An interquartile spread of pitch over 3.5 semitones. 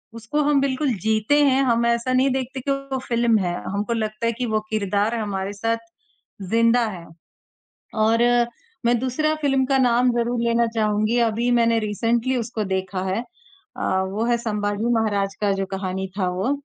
No: average, 3.0 semitones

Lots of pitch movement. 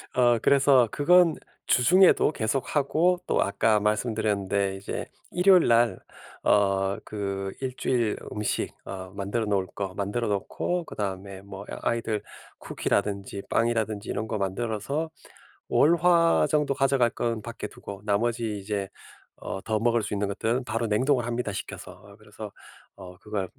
No: average, 3.9 semitones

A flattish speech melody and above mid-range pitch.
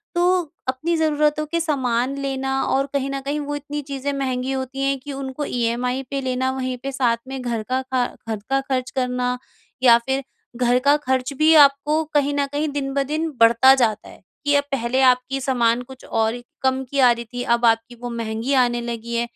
Yes: narrow, 2.3 semitones; very high, 265 Hz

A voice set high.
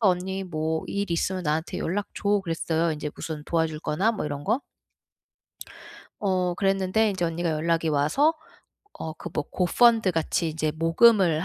No: medium, 170 Hz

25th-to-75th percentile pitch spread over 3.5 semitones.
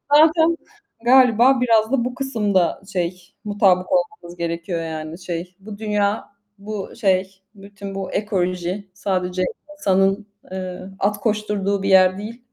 No: average, 2.9 semitones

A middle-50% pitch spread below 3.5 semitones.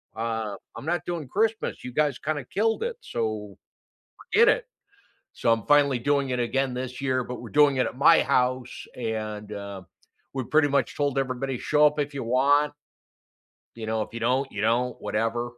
No: average, 4.0 semitones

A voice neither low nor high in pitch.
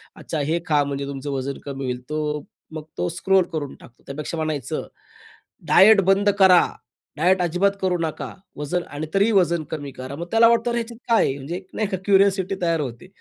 Yes: medium, 165 Hz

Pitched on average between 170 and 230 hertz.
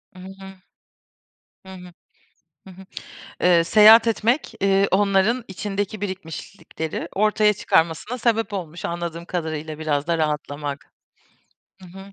Yes: high, 190 Hz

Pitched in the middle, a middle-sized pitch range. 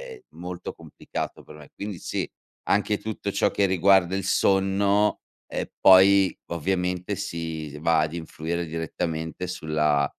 No: very low, 90 Hz; average, 3.2 semitones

